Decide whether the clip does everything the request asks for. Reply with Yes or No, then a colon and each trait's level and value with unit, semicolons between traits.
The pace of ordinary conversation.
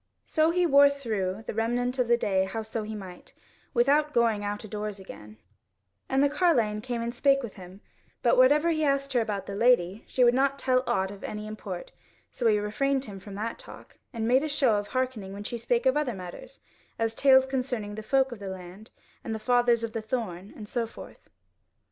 No: fast, 210 wpm